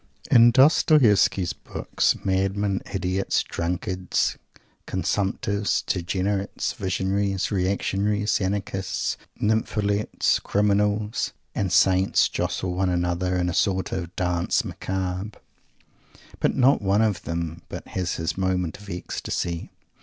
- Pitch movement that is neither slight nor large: No, narrow, 2.1 semitones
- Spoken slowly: Yes, slow, 105 wpm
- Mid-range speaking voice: No, very low, 95 Hz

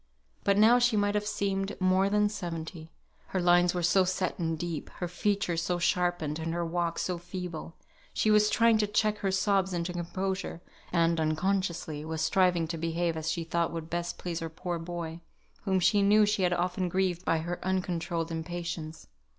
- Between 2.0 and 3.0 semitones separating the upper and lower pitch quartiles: Yes, narrow, 2.6 semitones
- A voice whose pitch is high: No, medium, 175 Hz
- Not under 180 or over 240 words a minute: Yes, average, 185 wpm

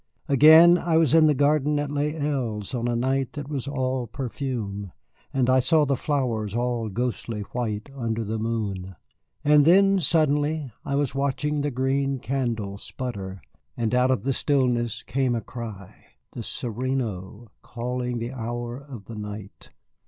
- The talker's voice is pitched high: No, low, 125 Hz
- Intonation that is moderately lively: Yes, average, 3.7 semitones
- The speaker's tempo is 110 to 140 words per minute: No, average, 160 wpm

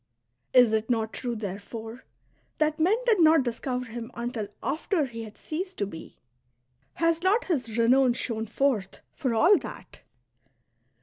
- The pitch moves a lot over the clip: Yes, wide, 5.7 semitones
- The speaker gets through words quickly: No, average, 150 wpm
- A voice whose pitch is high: Yes, high, 245 Hz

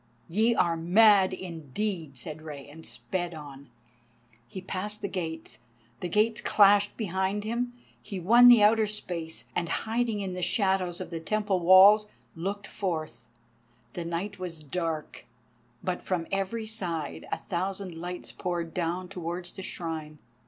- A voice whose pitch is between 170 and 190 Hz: Yes, medium, 185 Hz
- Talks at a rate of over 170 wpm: No, average, 145 wpm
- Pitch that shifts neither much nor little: Yes, average, 3.7 semitones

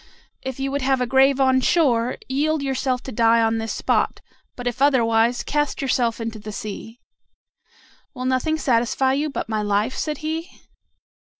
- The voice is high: Yes, very high, 255 Hz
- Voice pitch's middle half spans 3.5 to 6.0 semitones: No, average, 3.1 semitones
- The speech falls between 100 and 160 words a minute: No, average, 170 wpm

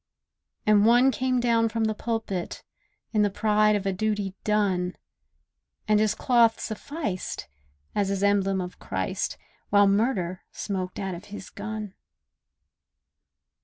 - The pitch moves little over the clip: Yes, narrow, 2.3 semitones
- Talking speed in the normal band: No, slow, 130 wpm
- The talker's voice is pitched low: No, high, 210 Hz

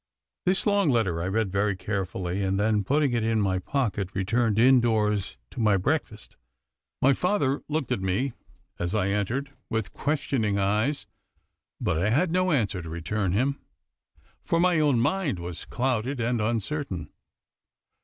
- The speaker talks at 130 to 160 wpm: Yes, average, 155 wpm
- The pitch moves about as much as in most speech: No, wide, 5.9 semitones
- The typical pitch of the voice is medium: No, low, 110 Hz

